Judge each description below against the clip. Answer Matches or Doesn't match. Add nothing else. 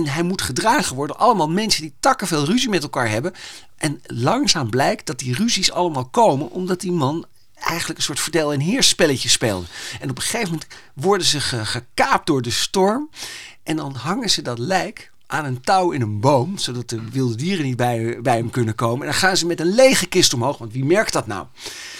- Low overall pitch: Doesn't match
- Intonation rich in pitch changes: Matches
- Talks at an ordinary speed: Doesn't match